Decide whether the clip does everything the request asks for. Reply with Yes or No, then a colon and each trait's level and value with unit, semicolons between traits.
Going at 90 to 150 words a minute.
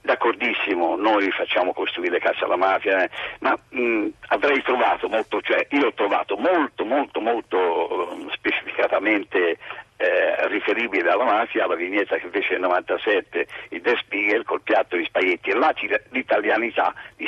Yes: average, 145 wpm